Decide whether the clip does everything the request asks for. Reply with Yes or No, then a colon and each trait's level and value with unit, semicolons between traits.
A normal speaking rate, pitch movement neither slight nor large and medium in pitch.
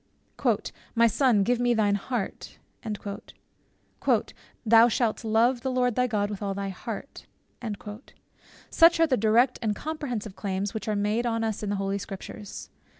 No: average, 150 wpm; average, 3.2 semitones; high, 225 Hz